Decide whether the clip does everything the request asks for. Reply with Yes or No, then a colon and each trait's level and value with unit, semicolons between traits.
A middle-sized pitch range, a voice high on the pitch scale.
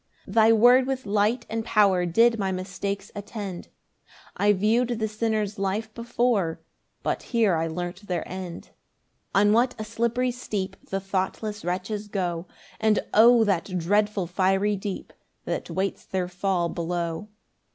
Yes: average, 3.0 semitones; high, 205 Hz